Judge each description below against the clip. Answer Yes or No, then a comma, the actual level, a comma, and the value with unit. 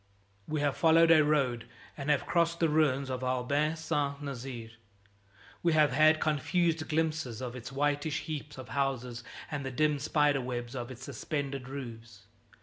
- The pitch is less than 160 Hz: Yes, medium, 140 Hz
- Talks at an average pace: Yes, average, 160 wpm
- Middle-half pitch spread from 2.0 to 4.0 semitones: Yes, average, 3.3 semitones